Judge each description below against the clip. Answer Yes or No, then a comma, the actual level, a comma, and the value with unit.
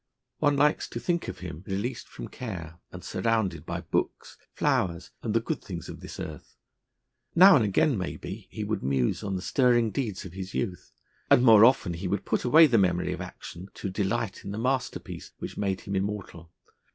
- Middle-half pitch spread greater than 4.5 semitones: Yes, average, 5.0 semitones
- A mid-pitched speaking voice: No, low, 100 Hz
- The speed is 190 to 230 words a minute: Yes, average, 195 wpm